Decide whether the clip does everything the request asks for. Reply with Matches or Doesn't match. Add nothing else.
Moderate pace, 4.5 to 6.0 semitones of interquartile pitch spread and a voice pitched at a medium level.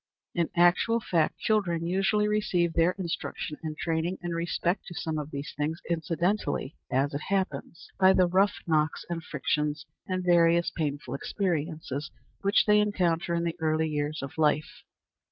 Doesn't match